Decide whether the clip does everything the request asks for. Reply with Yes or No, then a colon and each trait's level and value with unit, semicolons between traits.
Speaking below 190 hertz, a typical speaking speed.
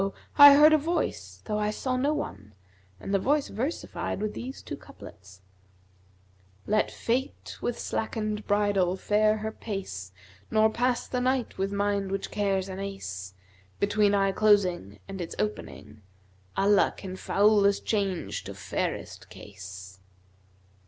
No: high, 200 Hz; average, 145 wpm